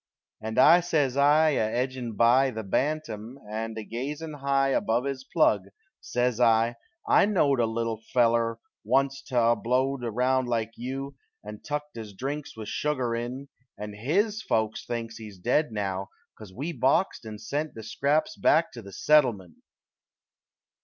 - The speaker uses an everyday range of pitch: Yes, average, 3.9 semitones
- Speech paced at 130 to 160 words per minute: Yes, average, 155 wpm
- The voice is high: No, low, 125 Hz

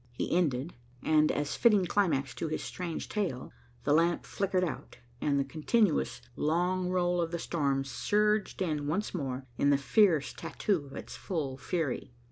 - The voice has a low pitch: No, medium, 165 Hz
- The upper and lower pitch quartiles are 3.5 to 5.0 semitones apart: Yes, average, 4.4 semitones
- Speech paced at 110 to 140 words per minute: No, average, 165 wpm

